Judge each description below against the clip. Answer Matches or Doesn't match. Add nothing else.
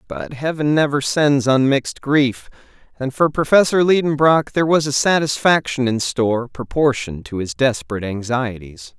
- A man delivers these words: Matches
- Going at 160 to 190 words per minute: Doesn't match